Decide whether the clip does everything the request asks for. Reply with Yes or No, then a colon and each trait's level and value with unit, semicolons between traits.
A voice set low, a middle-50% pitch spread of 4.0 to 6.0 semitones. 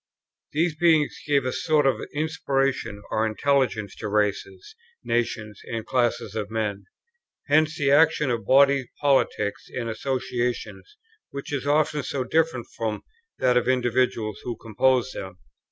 Yes: low, 130 Hz; average, 4.4 semitones